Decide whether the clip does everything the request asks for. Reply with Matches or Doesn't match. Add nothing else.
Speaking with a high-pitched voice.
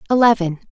Matches